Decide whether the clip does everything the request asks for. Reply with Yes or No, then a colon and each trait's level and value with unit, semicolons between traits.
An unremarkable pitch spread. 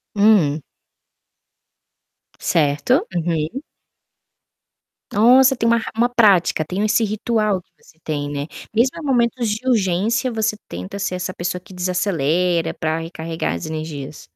No: wide, 6.1 semitones